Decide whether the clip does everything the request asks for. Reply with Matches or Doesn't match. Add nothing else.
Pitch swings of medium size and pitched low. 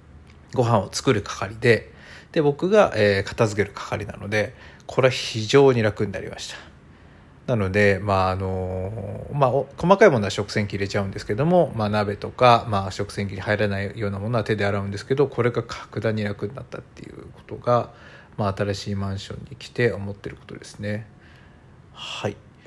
Matches